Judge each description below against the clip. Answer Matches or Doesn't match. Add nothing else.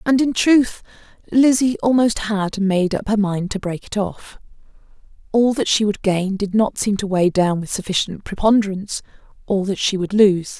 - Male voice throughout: Doesn't match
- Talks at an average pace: Matches